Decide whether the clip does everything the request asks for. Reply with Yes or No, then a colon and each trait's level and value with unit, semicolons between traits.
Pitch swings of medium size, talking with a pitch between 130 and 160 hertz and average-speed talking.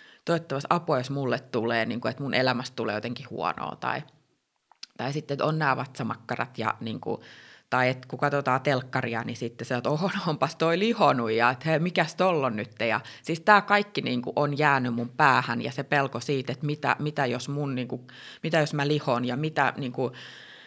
No: average, 3.6 semitones; low, 135 Hz; fast, 205 wpm